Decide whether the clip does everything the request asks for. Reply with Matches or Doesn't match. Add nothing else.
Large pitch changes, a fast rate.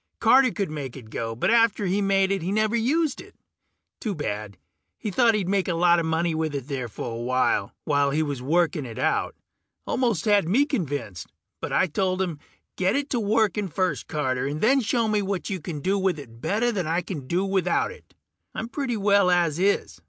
Matches